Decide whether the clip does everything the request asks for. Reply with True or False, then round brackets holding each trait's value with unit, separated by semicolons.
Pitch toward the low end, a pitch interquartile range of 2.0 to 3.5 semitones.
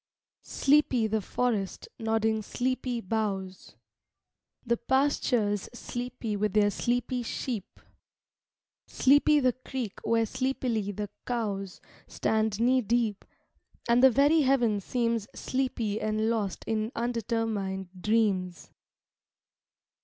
False (225 Hz; 3.1 semitones)